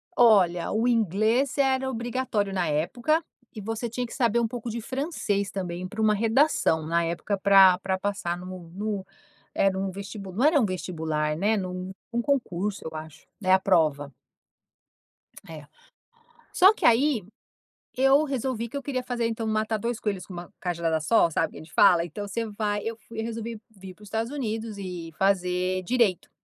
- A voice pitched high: Yes, high, 205 Hz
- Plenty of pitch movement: No, average, 4.3 semitones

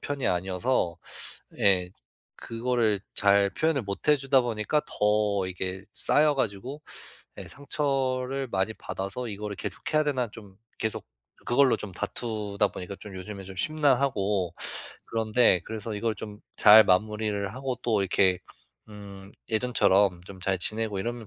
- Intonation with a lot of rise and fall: No, average, 4.4 semitones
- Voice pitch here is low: Yes, low, 105 Hz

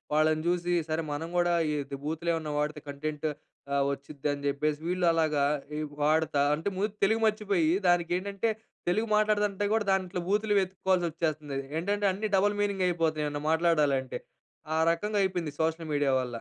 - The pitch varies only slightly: No, average, 4.3 semitones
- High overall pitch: No, medium, 170 Hz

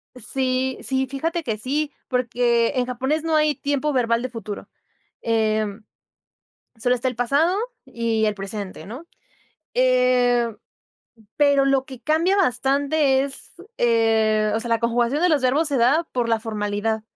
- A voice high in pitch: Yes, very high, 250 Hz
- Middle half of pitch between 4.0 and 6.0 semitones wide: No, average, 3.5 semitones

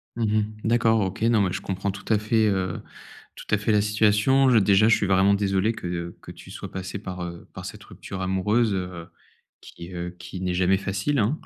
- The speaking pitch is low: Yes, low, 100 Hz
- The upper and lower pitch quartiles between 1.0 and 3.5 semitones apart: Yes, average, 2.8 semitones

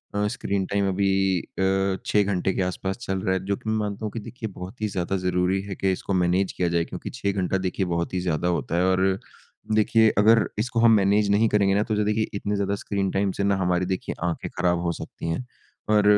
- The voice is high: No, very low, 95 Hz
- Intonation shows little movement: Yes, narrow, 2.0 semitones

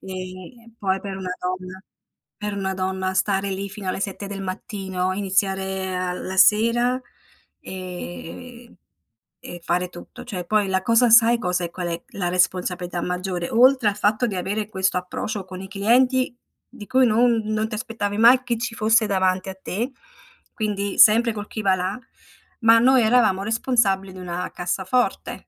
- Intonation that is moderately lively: Yes, average, 3.5 semitones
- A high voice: Yes, high, 195 Hz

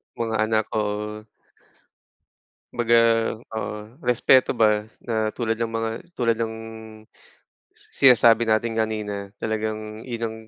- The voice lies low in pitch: Yes, low, 110 Hz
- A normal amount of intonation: No, narrow, 1.3 semitones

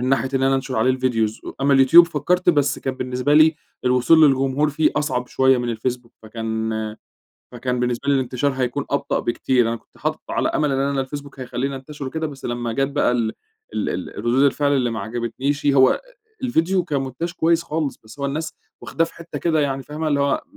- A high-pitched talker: No, low, 135 Hz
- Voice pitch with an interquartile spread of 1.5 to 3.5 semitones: Yes, average, 2.9 semitones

